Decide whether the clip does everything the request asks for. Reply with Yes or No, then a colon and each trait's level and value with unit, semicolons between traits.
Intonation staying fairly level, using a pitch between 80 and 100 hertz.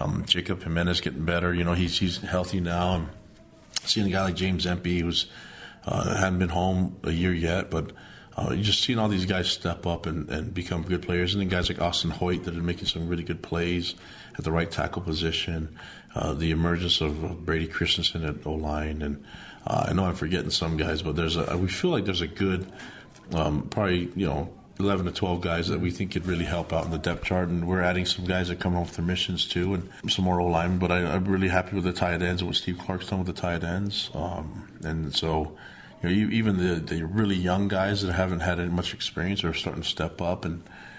Yes: narrow, 1.8 semitones; very low, 90 Hz